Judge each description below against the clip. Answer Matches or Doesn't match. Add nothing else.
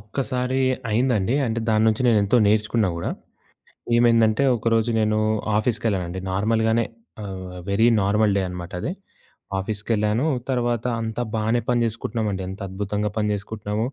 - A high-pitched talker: Doesn't match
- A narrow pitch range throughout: Matches